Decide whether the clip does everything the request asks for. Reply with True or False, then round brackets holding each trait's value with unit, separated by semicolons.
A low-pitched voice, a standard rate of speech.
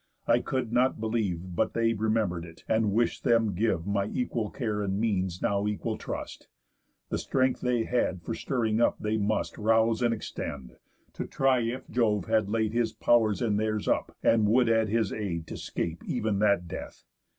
True (110 Hz; 185 wpm)